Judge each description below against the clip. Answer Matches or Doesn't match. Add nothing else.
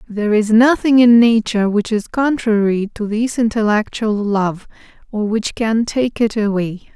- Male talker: Doesn't match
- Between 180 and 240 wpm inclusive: Doesn't match